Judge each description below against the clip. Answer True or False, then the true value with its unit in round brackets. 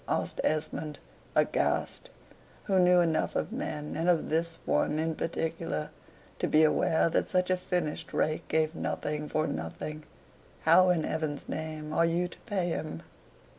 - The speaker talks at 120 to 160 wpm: True (155 wpm)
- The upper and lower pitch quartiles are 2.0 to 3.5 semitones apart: True (2.4 semitones)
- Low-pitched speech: False (160 Hz)